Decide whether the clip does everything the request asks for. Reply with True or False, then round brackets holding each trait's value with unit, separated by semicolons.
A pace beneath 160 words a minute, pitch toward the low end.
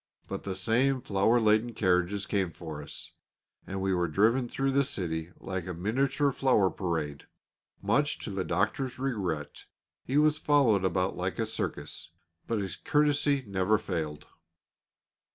True (150 wpm; 100 Hz)